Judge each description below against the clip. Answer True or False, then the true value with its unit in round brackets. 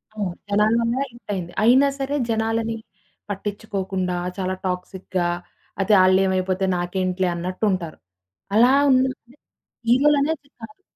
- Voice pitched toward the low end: False (205 Hz)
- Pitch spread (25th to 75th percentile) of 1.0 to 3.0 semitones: False (4.1 semitones)